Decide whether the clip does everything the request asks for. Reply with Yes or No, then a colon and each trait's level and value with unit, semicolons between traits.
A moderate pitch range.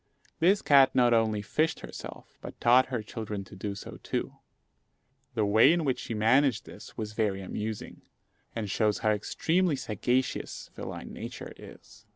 Yes: average, 3.8 semitones